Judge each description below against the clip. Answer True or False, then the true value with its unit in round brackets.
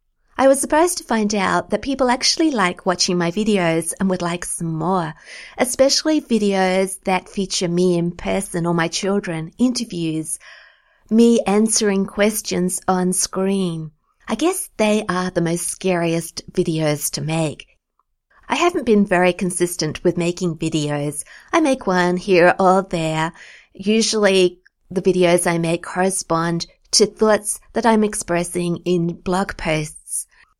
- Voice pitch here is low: False (185 Hz)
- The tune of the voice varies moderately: True (3.5 semitones)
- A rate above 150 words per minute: False (140 wpm)